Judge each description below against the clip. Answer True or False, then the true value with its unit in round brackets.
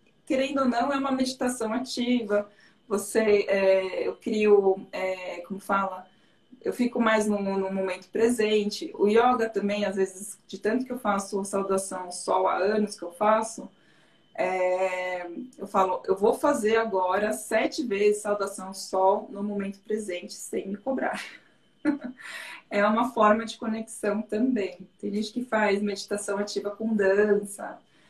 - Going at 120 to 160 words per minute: True (150 wpm)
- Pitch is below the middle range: False (205 Hz)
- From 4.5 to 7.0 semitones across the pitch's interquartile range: False (2.5 semitones)